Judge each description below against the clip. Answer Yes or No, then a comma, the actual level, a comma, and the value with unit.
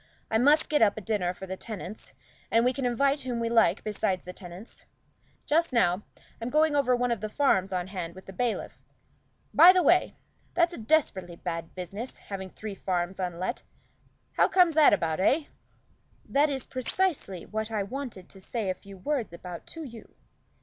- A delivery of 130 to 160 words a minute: No, average, 185 wpm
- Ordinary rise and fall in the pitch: No, wide, 6.6 semitones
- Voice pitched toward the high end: Yes, high, 220 Hz